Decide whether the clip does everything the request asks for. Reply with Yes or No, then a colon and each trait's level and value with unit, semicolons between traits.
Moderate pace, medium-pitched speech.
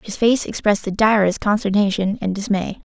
No: average, 165 wpm; high, 205 Hz